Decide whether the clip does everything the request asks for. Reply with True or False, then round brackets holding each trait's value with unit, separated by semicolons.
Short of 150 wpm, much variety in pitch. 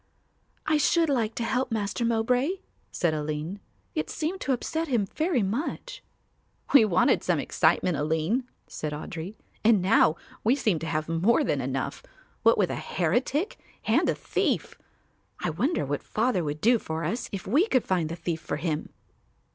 False (170 wpm; 7.9 semitones)